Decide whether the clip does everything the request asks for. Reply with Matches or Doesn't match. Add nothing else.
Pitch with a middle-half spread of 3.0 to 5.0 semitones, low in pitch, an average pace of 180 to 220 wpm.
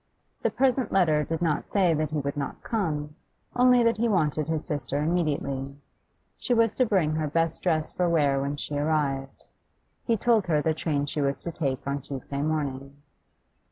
Doesn't match